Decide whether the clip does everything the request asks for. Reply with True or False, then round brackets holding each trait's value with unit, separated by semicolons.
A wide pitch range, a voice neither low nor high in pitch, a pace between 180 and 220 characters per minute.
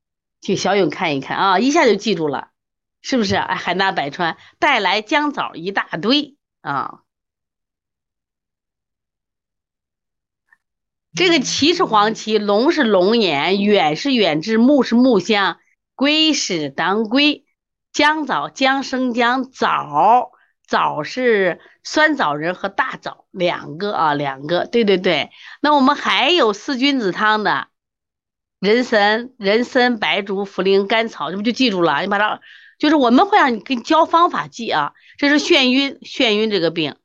False (6.3 semitones; 225 Hz; 205 characters per minute)